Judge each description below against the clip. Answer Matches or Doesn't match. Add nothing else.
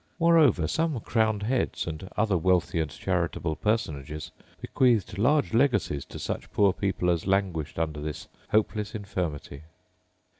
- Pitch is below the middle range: Matches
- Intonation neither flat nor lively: Doesn't match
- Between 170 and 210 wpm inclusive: Doesn't match